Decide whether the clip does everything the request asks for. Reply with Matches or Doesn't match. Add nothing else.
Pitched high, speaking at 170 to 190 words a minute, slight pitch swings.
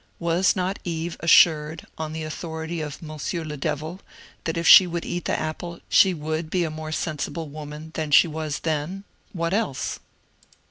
Doesn't match